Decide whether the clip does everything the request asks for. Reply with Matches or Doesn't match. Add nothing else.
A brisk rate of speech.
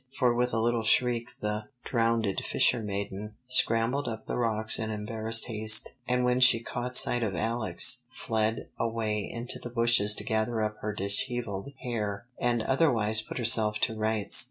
Doesn't match